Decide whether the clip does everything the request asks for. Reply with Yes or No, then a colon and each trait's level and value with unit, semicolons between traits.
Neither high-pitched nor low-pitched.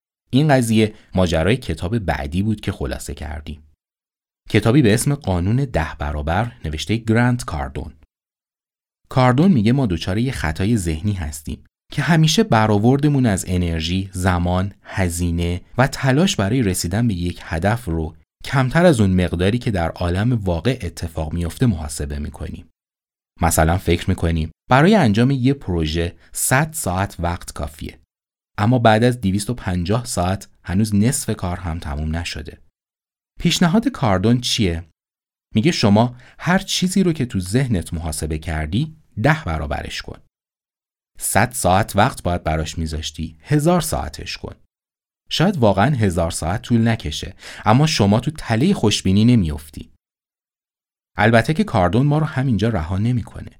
No: very low, 95 Hz